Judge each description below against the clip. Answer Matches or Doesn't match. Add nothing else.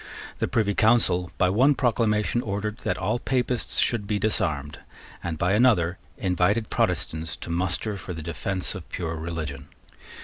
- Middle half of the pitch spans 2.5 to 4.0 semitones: Doesn't match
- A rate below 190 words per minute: Matches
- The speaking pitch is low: Matches